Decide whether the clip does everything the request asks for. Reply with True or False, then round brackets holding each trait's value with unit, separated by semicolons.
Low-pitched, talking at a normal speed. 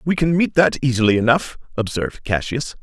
True (130 Hz; 170 wpm)